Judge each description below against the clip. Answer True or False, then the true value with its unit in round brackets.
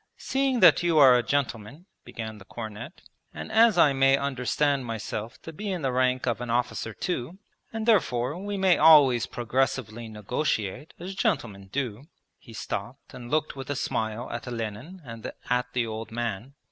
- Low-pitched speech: True (125 Hz)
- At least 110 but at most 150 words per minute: False (170 wpm)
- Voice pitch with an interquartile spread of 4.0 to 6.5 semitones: True (5.2 semitones)